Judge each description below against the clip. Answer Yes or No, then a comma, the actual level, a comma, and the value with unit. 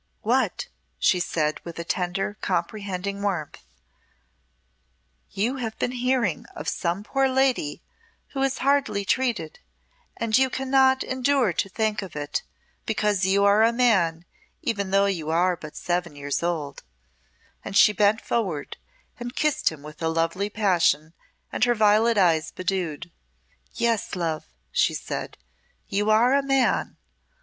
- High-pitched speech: Yes, high, 200 Hz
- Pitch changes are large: Yes, wide, 5.8 semitones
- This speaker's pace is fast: No, average, 140 wpm